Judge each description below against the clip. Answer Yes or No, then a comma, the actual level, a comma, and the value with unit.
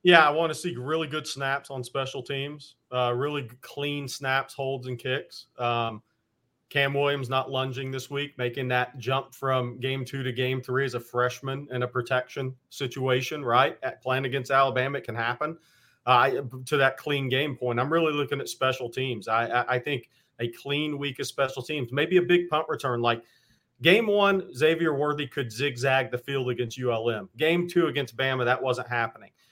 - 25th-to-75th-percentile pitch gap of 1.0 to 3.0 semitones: Yes, narrow, 2.4 semitones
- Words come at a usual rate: Yes, average, 190 wpm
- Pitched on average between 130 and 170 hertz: Yes, low, 135 Hz